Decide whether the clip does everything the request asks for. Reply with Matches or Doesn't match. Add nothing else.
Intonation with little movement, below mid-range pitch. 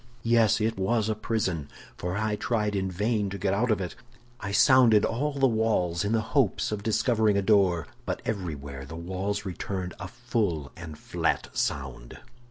Doesn't match